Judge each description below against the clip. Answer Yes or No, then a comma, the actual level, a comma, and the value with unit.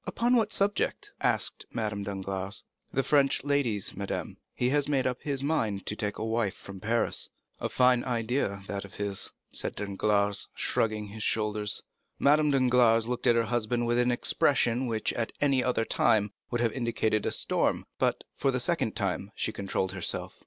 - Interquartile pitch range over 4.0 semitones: No, average, 3.7 semitones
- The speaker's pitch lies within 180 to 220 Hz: No, low, 115 Hz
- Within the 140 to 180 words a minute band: Yes, average, 175 wpm